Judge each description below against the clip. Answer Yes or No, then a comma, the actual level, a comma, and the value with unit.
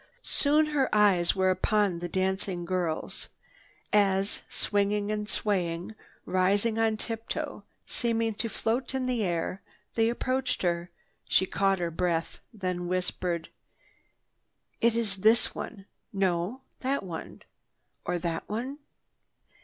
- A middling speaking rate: No, slow, 120 wpm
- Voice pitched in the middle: No, high, 200 Hz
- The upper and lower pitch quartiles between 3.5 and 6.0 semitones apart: Yes, average, 4.0 semitones